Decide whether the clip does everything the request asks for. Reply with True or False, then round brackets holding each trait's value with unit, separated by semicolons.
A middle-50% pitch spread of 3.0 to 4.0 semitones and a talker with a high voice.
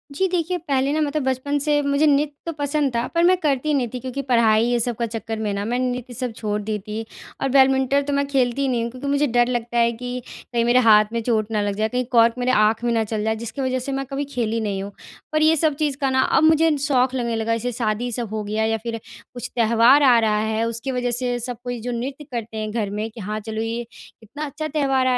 True (3.5 semitones; 245 Hz)